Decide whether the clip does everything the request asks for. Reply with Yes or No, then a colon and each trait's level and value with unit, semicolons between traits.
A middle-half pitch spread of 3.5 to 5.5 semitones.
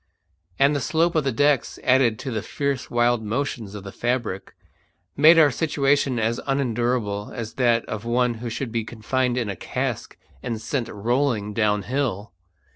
Yes: average, 3.8 semitones